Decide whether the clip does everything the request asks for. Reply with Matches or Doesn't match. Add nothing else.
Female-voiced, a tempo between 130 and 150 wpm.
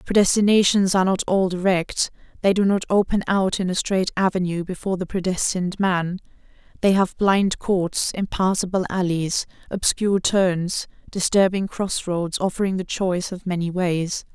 Matches